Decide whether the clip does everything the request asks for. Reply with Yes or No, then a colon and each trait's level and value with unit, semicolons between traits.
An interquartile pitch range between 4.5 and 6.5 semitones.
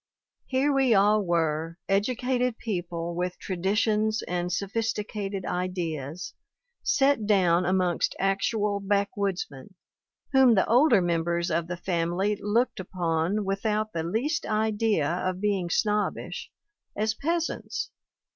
No: average, 3.8 semitones